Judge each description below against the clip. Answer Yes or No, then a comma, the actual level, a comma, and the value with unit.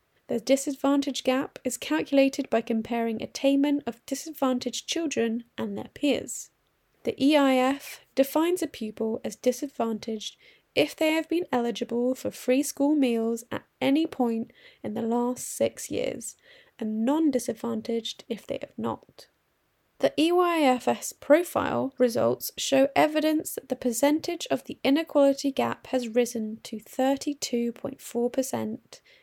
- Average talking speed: No, slow, 125 wpm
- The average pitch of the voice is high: Yes, very high, 265 Hz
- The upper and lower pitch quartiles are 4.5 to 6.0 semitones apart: No, average, 3.5 semitones